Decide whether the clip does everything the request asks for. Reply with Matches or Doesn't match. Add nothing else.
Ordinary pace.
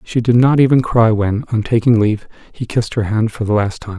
Doesn't match